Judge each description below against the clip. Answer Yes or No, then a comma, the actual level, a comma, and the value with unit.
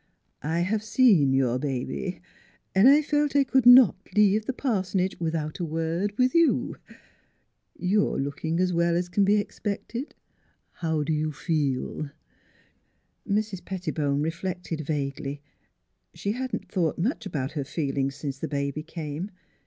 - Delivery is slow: No, average, 155 wpm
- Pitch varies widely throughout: Yes, wide, 5.8 semitones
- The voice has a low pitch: No, medium, 170 Hz